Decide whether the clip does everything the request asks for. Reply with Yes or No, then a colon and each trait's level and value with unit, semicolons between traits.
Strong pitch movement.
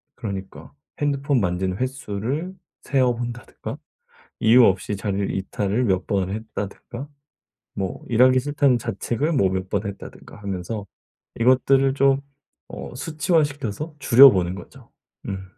Yes: wide, 5.7 semitones